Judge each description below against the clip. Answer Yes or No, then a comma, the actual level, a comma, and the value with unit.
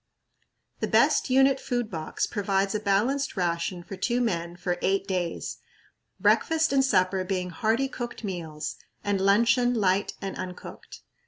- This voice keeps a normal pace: Yes, average, 145 wpm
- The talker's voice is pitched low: No, high, 195 Hz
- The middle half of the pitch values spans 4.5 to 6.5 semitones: Yes, average, 4.9 semitones